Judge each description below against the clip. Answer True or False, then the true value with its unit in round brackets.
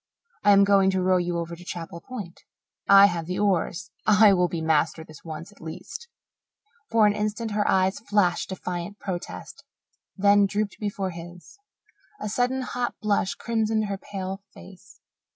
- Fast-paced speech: False (165 wpm)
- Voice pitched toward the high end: True (195 Hz)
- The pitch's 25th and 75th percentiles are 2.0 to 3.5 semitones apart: True (3.0 semitones)